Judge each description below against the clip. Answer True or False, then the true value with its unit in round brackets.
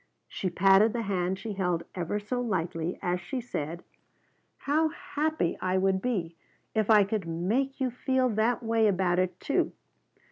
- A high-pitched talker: True (195 Hz)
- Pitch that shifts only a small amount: False (5.0 semitones)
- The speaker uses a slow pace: False (165 wpm)